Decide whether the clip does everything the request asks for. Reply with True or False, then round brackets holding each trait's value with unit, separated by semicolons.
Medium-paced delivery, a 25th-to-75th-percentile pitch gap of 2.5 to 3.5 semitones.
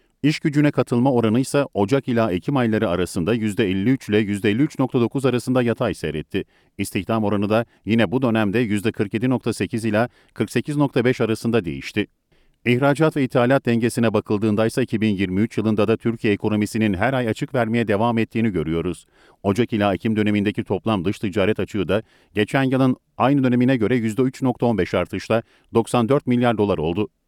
False (145 wpm; 3.2 semitones)